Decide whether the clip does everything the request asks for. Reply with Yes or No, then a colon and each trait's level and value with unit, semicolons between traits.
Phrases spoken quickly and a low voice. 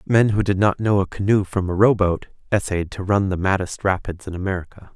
Yes: fast, 230 wpm; very low, 95 Hz